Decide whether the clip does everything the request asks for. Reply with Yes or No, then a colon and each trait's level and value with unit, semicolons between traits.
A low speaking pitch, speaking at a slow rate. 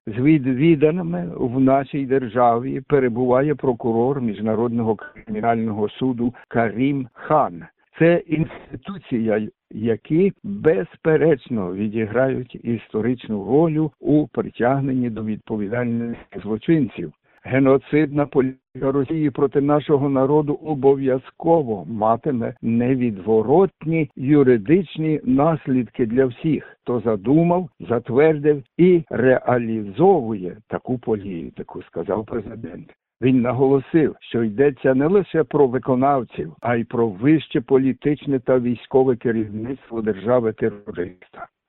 Yes: low, 130 Hz; slow, 90 wpm